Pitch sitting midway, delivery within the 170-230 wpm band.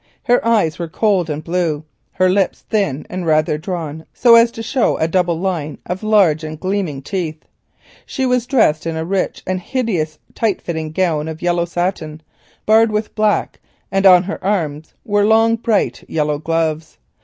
Yes: medium, 180 Hz; average, 175 wpm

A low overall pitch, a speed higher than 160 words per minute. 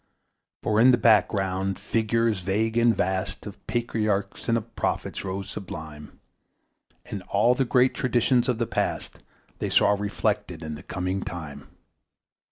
No: low, 105 Hz; average, 145 wpm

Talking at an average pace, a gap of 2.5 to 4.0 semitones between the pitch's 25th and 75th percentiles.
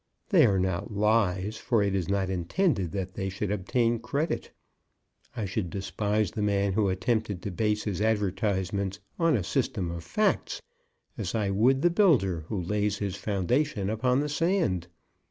Yes: average, 165 wpm; average, 3.0 semitones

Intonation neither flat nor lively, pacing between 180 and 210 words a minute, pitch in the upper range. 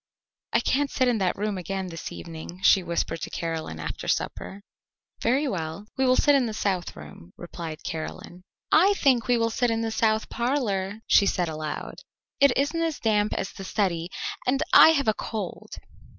No: wide, 6.4 semitones; average, 185 wpm; high, 210 Hz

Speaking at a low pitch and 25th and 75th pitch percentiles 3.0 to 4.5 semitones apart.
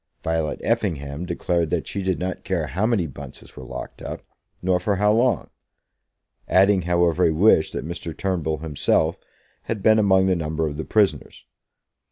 Yes: very low, 90 Hz; average, 3.4 semitones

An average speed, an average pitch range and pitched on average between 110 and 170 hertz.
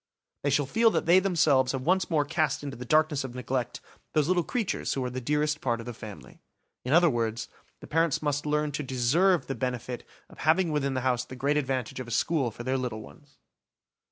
No: fast, 220 wpm; average, 3.6 semitones; medium, 140 Hz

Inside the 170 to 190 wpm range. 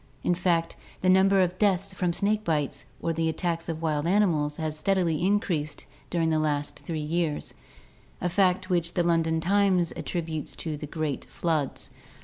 Yes: average, 175 wpm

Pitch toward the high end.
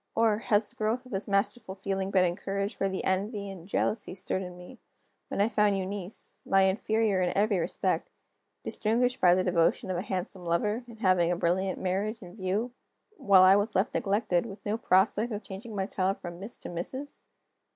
Yes: high, 195 Hz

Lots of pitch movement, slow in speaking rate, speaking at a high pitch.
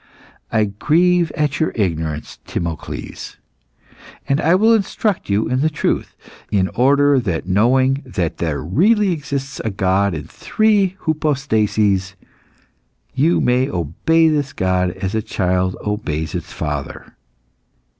No: wide, 8.5 semitones; slow, 125 wpm; low, 115 Hz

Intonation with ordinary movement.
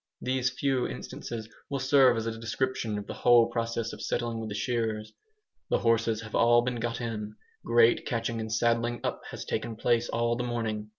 No: narrow, 1.1 semitones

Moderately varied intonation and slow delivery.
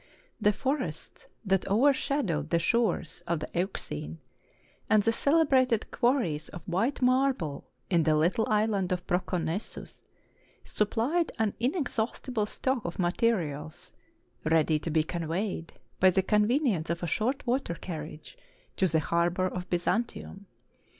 No: wide, 6.0 semitones; slow, 130 wpm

